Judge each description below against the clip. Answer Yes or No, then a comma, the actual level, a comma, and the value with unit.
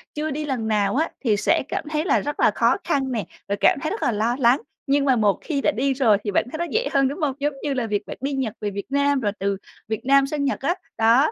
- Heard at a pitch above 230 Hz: Yes, very high, 270 Hz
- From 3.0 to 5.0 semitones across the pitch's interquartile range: Yes, average, 4.5 semitones